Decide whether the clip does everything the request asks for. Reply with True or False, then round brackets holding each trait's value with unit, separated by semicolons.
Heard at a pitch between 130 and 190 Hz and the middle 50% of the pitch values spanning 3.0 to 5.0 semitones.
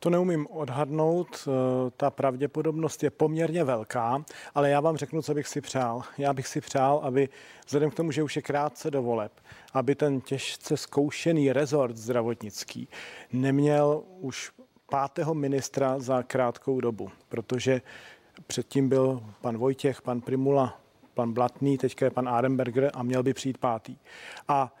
False (135 Hz; 2.6 semitones)